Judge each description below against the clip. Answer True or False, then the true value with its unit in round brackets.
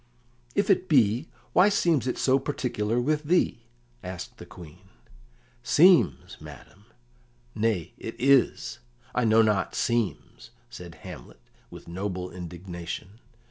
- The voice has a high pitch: False (115 Hz)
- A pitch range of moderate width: False (6.9 semitones)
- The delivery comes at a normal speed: False (120 wpm)